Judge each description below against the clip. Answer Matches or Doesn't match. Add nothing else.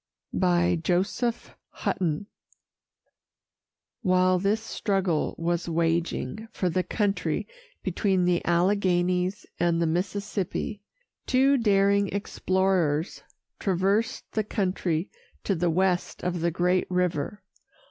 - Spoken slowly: Matches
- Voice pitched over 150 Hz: Matches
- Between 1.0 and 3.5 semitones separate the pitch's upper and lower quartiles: Matches